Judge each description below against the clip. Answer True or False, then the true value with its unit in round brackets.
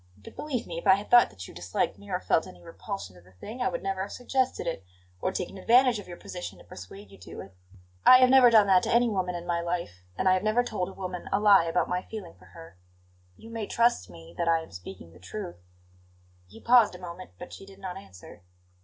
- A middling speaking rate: False (255 wpm)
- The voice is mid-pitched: True (180 Hz)